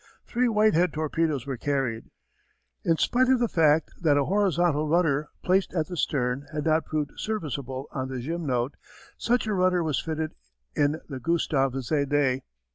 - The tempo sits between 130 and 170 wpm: Yes, average, 160 wpm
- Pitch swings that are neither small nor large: Yes, average, 4.1 semitones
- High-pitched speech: No, medium, 155 Hz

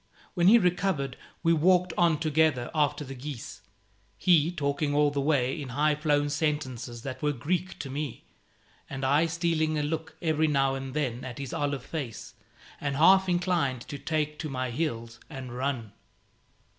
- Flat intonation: No, average, 3.2 semitones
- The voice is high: No, medium, 145 Hz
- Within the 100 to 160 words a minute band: No, average, 170 wpm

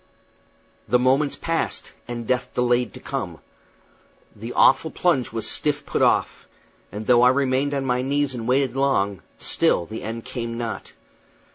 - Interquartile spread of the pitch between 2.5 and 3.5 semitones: Yes, average, 2.9 semitones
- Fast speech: No, average, 155 wpm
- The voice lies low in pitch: Yes, low, 125 Hz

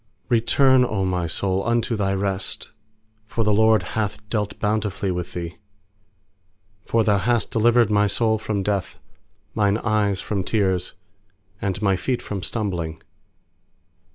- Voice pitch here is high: No, low, 105 Hz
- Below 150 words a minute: Yes, slow, 135 wpm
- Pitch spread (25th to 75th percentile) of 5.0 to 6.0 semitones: No, narrow, 2.5 semitones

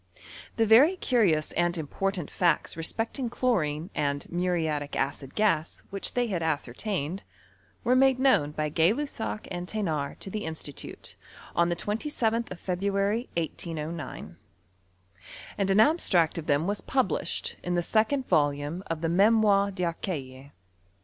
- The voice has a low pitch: No, medium, 180 Hz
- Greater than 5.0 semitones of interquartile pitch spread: Yes, wide, 5.6 semitones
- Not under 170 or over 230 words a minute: No, slow, 135 wpm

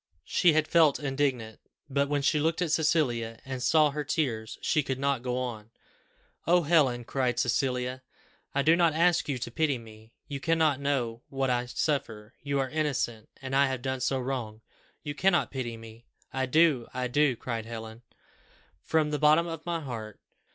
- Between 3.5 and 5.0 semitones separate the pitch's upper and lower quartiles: Yes, average, 3.9 semitones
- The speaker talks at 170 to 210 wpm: Yes, average, 180 wpm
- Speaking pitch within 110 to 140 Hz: Yes, low, 135 Hz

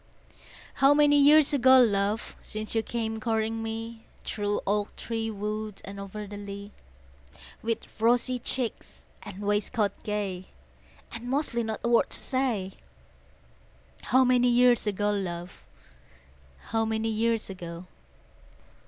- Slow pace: Yes, slow, 125 wpm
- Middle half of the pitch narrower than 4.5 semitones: Yes, narrow, 2.6 semitones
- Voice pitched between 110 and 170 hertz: No, high, 220 Hz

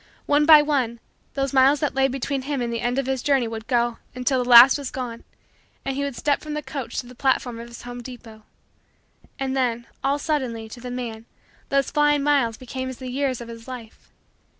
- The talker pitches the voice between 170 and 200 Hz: No, very high, 260 Hz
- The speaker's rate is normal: No, fast, 220 wpm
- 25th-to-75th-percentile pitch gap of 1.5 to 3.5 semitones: Yes, average, 2.7 semitones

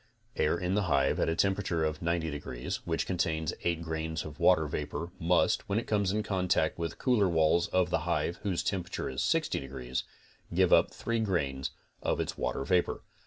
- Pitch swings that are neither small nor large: Yes, average, 3.1 semitones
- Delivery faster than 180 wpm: Yes, average, 195 wpm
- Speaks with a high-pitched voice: No, very low, 85 Hz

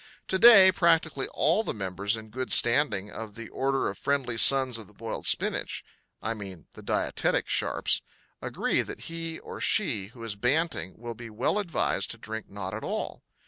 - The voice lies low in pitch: Yes, low, 115 Hz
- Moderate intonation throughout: No, wide, 6.4 semitones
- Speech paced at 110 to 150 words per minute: No, average, 185 wpm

